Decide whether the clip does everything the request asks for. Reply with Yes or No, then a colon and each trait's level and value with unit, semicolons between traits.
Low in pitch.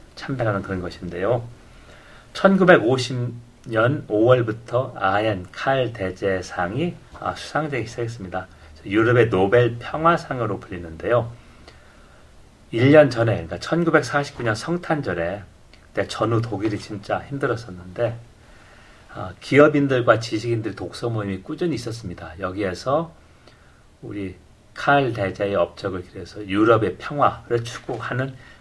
Yes: low, 115 Hz